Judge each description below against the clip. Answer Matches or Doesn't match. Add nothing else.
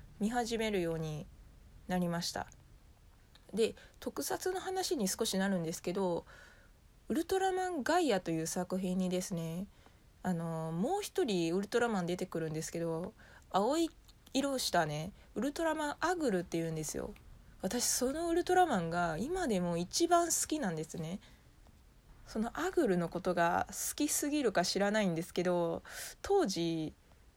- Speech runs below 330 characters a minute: Matches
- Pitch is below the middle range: Doesn't match